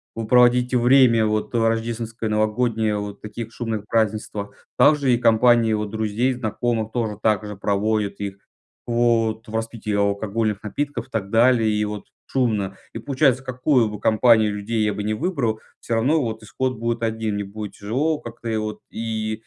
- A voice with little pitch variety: Yes, narrow, 2.0 semitones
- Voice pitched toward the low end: Yes, low, 110 Hz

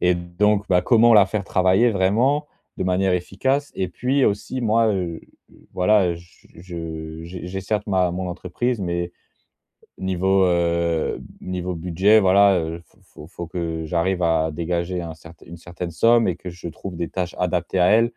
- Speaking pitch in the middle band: No, very low, 90 Hz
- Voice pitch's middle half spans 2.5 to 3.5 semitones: Yes, average, 2.8 semitones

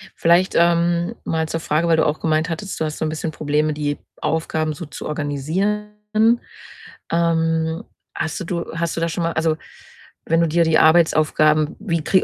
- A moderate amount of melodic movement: No, narrow, 1.4 semitones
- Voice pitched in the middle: Yes, medium, 160 Hz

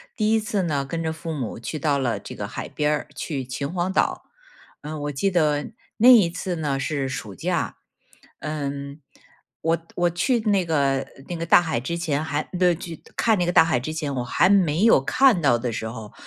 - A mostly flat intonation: No, average, 4.1 semitones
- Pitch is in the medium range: Yes, medium, 155 Hz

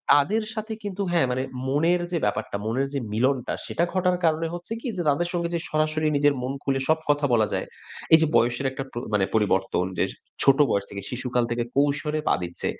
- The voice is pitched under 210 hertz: Yes, medium, 140 Hz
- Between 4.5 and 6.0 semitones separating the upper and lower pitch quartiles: Yes, wide, 5.4 semitones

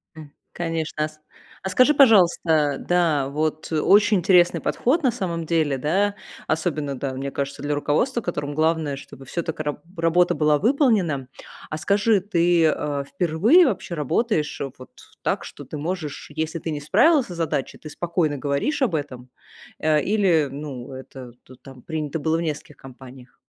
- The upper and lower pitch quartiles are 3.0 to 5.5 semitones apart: Yes, average, 3.6 semitones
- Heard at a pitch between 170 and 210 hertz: No, medium, 155 Hz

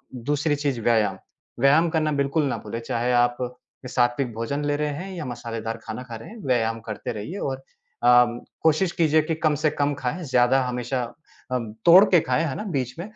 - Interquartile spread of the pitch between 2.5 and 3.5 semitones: No, average, 4.2 semitones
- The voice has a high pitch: No, low, 130 Hz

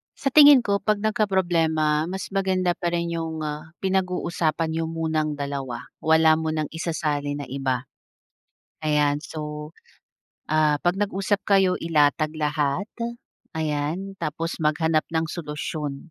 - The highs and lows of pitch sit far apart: No, average, 3.3 semitones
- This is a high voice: No, medium, 160 Hz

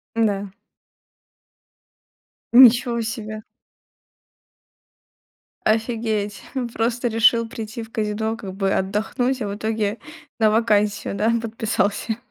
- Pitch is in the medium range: No, high, 220 Hz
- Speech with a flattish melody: Yes, narrow, 1.7 semitones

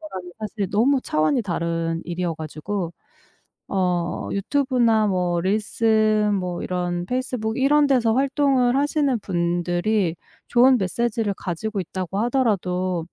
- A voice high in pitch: Yes, high, 205 Hz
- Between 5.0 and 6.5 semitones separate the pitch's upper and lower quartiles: Yes, wide, 5.5 semitones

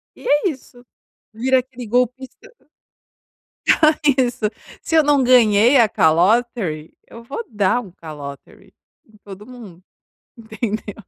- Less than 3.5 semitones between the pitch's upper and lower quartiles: No, average, 3.9 semitones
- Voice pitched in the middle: No, high, 230 Hz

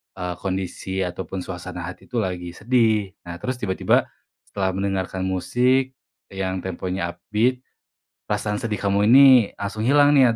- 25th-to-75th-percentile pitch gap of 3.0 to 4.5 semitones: Yes, average, 3.8 semitones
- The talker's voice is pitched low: Yes, very low, 95 Hz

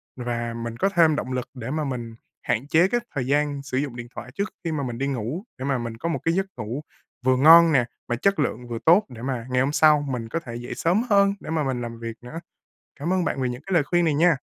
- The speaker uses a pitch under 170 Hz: Yes, low, 135 Hz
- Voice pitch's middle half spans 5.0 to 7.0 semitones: Yes, average, 5.3 semitones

